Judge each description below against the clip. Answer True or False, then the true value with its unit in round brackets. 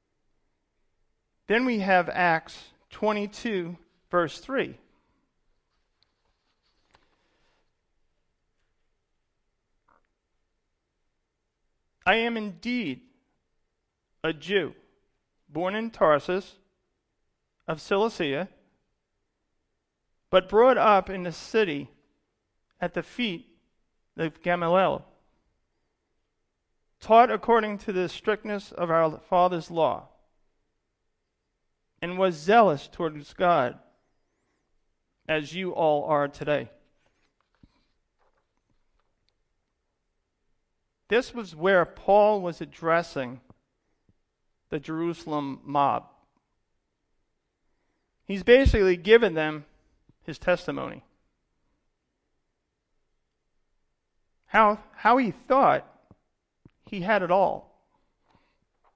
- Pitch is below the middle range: False (185 Hz)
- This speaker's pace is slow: True (70 wpm)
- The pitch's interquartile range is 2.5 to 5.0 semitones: True (4.7 semitones)